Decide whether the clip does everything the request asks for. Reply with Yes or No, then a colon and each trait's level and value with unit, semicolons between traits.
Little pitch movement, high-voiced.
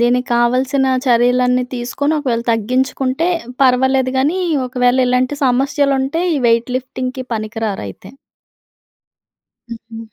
Yes: narrow, 1.8 semitones; very high, 250 Hz